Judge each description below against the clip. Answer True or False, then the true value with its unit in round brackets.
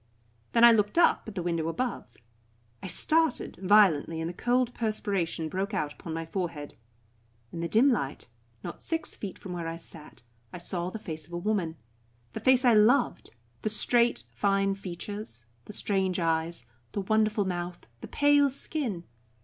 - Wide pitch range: False (4.8 semitones)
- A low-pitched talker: False (190 Hz)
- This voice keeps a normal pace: True (170 wpm)